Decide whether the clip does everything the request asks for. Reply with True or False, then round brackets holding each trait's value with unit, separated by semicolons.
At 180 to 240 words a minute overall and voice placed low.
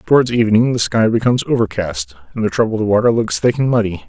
True (205 wpm; 110 Hz)